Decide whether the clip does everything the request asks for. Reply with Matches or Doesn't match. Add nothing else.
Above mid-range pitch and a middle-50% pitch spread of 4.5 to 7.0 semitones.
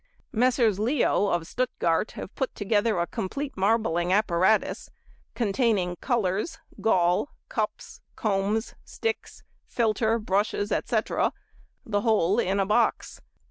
Doesn't match